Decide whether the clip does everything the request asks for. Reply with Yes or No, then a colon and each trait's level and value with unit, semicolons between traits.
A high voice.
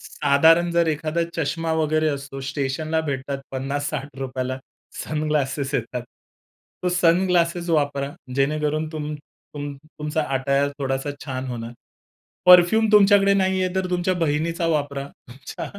No: medium, 150 Hz